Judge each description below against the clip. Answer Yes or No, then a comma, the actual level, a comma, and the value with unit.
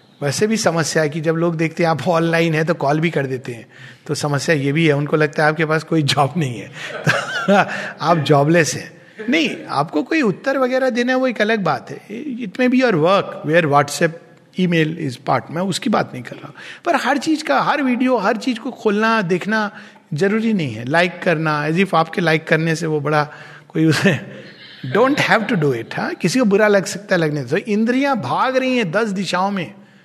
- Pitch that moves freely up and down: Yes, wide, 5.9 semitones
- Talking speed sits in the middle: No, fast, 230 wpm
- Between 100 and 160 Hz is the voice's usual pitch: No, medium, 170 Hz